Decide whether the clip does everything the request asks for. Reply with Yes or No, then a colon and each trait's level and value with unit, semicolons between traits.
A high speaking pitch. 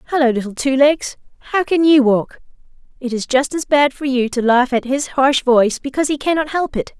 Yes: very high, 270 Hz